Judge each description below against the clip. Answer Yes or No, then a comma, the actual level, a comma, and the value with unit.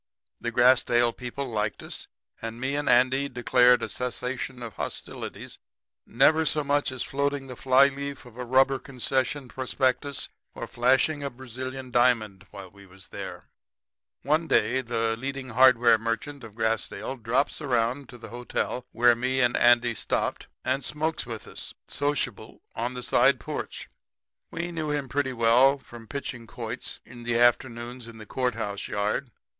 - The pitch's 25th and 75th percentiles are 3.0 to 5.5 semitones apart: No, narrow, 2.4 semitones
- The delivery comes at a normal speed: Yes, average, 160 wpm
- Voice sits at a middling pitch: No, low, 125 Hz